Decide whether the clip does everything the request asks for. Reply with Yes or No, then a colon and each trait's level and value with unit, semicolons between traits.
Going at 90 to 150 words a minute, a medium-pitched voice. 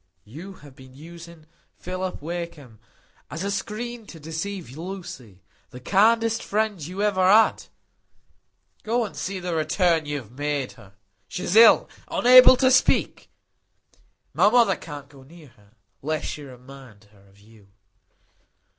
Yes: average, 140 wpm; medium, 165 Hz